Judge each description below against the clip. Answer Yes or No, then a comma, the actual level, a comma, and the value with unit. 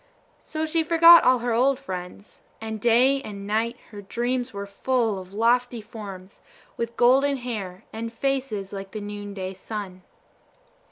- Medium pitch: No, high, 225 Hz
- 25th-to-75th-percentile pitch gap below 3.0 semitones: No, average, 4.0 semitones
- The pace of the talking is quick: No, average, 150 wpm